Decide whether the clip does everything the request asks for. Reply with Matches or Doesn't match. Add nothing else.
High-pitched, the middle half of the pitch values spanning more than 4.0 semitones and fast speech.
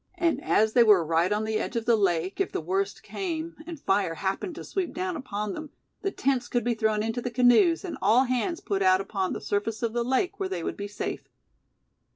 Matches